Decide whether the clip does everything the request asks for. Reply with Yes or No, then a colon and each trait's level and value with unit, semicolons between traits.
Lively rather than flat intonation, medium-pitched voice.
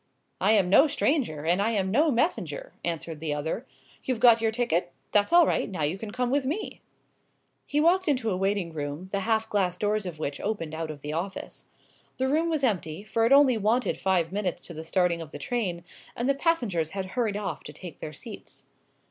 No: wide, 6.5 semitones; high, 205 Hz